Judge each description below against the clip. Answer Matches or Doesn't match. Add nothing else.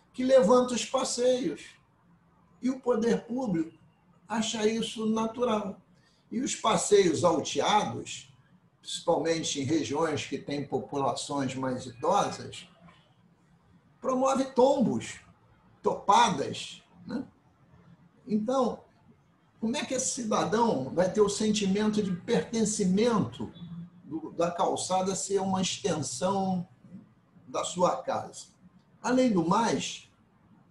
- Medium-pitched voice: Doesn't match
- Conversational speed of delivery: Doesn't match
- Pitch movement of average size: Doesn't match